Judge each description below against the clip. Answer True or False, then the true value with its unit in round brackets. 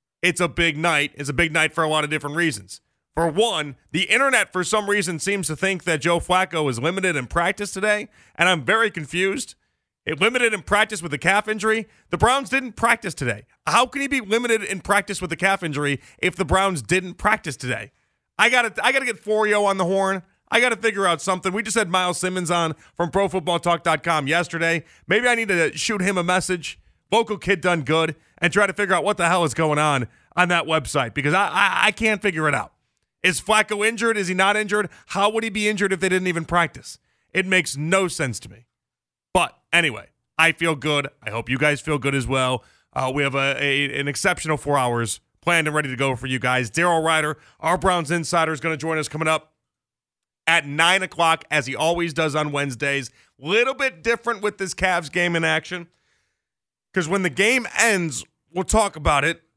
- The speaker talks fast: True (220 wpm)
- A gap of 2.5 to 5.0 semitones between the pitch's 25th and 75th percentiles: True (4.6 semitones)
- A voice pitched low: False (175 Hz)